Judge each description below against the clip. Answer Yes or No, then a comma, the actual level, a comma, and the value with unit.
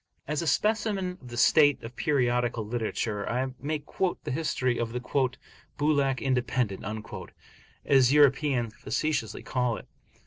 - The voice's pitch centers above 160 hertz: No, low, 130 Hz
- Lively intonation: No, average, 3.7 semitones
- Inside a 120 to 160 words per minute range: Yes, slow, 135 wpm